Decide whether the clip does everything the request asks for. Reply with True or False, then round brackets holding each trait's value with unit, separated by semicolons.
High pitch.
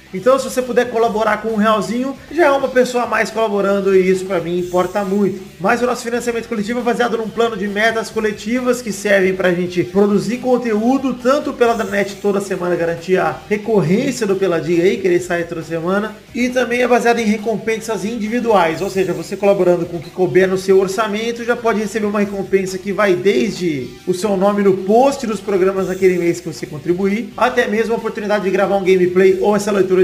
True (205 Hz)